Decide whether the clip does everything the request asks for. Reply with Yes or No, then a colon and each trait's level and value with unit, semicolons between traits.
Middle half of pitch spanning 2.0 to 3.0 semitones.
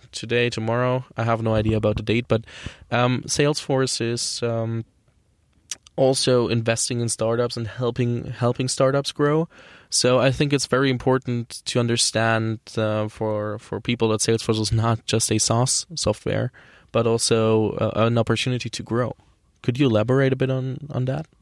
Yes: narrow, 2.4 semitones